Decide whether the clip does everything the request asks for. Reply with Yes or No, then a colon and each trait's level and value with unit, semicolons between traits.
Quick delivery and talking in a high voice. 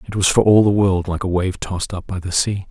No: fast, 310 wpm; very low, 95 Hz